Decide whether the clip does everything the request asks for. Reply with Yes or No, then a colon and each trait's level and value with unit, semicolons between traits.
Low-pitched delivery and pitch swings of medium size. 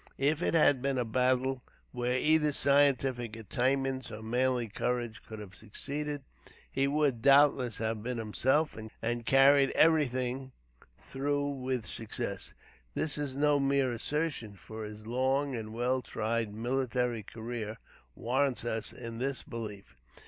Yes: low, 125 Hz; average, 3.3 semitones